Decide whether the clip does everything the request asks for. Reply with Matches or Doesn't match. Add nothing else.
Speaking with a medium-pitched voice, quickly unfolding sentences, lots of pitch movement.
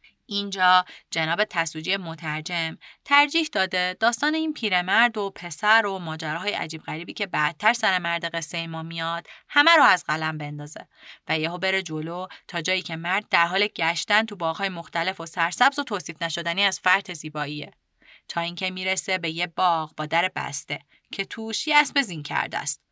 Doesn't match